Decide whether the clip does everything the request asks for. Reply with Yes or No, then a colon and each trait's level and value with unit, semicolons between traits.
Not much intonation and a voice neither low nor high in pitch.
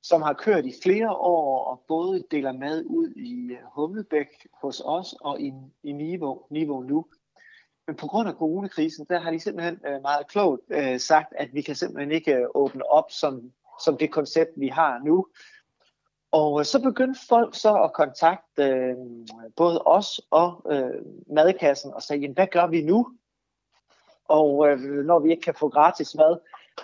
No: average, 3.8 semitones; medium, 155 Hz